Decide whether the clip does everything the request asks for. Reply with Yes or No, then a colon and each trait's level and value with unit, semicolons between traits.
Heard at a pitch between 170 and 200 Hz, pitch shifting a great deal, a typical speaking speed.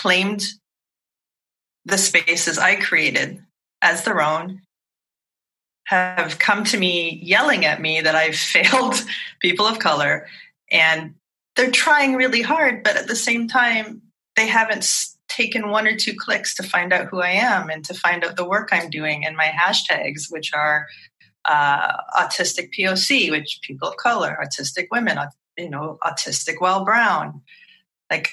Yes: medium, 185 Hz; wide, 6.1 semitones; average, 155 wpm